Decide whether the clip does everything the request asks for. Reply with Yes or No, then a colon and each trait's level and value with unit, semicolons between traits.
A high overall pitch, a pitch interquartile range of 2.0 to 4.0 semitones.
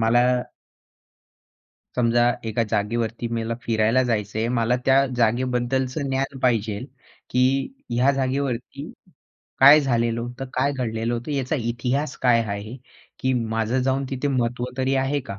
No: low, 125 Hz; narrow, 2.5 semitones